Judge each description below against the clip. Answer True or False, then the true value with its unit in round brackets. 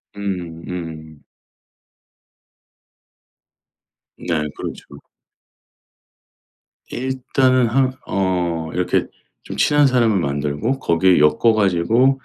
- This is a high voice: False (95 Hz)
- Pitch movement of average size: False (7.4 semitones)